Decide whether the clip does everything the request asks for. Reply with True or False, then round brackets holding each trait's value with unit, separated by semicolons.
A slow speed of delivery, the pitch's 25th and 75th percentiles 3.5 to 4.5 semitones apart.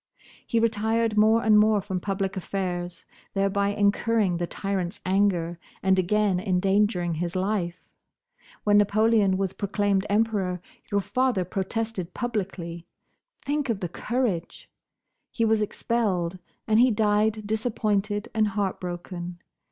False (120 wpm; 2.9 semitones)